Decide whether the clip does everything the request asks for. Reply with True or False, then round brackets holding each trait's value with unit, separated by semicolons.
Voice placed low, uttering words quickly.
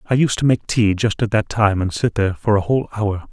True (105 Hz; 290 wpm)